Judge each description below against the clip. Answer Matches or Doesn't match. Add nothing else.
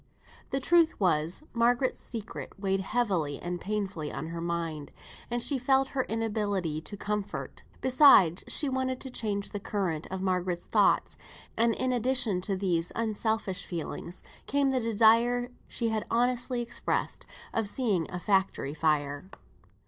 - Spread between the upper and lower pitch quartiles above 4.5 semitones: Matches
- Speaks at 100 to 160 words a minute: Matches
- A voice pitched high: Matches